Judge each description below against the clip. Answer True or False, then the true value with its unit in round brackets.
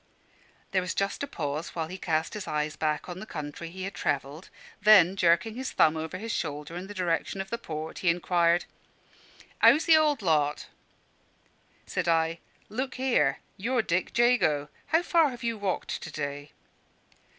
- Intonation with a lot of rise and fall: True (5.7 semitones)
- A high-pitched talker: False (175 Hz)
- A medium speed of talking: True (175 wpm)